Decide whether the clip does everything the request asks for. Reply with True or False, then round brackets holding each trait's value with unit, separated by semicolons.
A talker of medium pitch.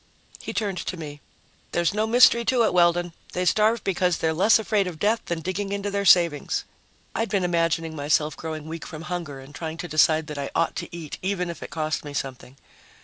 True (170 Hz)